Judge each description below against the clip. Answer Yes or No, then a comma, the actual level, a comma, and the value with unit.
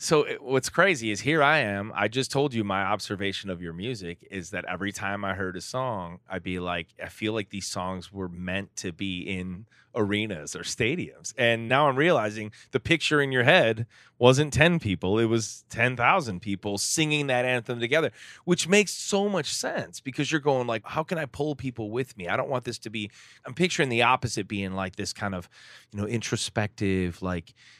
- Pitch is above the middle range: No, low, 110 Hz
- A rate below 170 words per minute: No, fast, 205 wpm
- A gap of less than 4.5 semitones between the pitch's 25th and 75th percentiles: No, average, 5.2 semitones